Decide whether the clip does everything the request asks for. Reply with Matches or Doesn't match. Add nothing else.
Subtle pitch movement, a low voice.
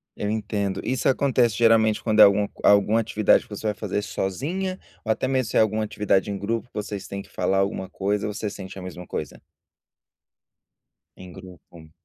Matches